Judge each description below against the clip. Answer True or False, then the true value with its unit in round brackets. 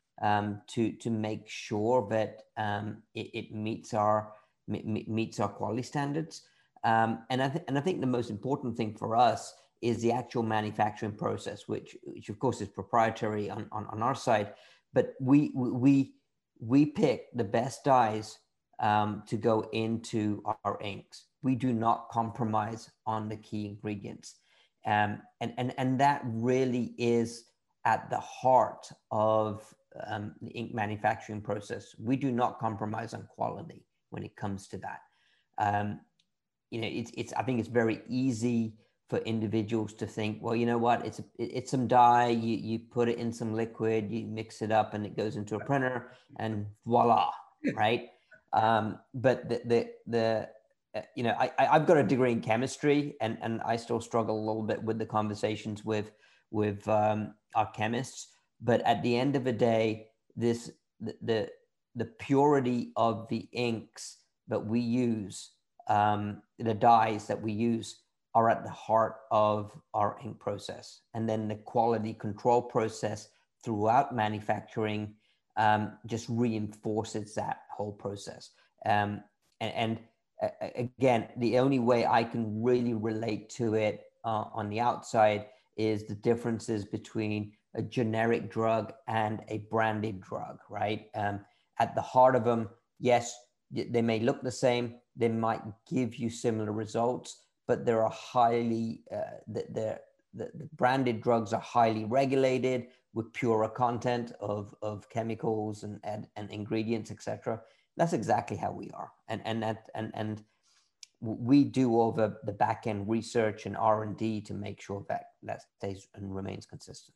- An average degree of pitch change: False (2.0 semitones)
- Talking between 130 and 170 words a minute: True (165 wpm)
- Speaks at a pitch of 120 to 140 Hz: False (110 Hz)